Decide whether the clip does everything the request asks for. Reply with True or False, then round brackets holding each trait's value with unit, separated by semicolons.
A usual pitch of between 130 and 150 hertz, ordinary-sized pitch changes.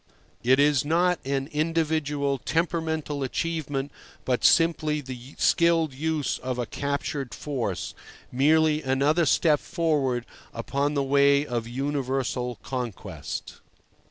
True (140 Hz; 3.2 semitones)